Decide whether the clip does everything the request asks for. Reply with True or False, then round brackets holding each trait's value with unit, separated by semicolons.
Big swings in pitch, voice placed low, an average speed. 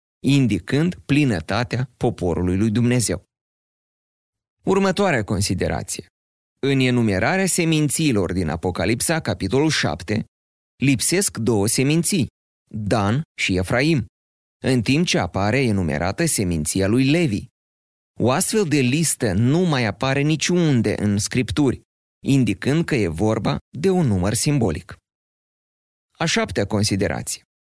False (7.4 semitones; 115 Hz; 105 wpm)